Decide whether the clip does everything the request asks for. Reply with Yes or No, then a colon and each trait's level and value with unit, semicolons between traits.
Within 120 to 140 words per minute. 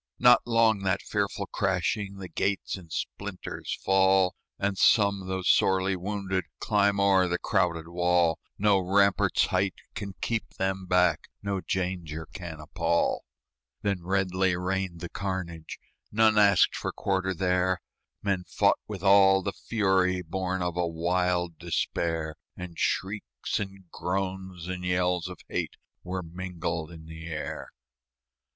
Yes: slow, 135 wpm